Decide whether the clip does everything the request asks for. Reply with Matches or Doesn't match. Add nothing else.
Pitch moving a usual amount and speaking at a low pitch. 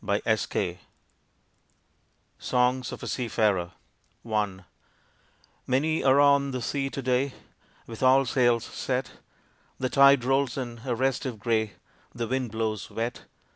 Matches